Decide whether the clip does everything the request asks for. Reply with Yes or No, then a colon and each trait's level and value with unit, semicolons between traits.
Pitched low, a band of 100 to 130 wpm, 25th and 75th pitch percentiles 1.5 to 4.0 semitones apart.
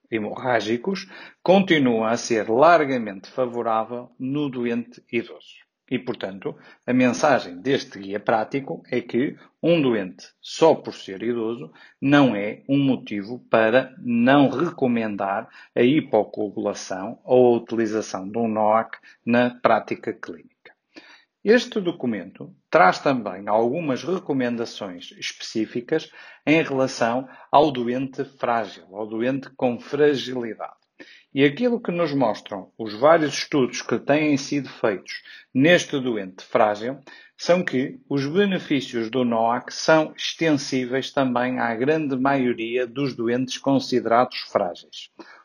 Yes: low, 125 Hz; slow, 120 wpm; average, 3.7 semitones